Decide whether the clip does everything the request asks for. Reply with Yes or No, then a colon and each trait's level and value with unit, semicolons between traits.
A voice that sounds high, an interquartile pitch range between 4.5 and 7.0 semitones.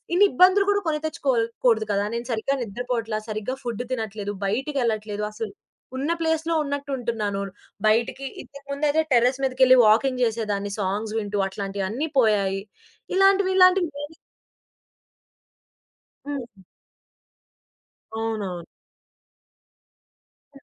Yes: high, 235 Hz; average, 5.1 semitones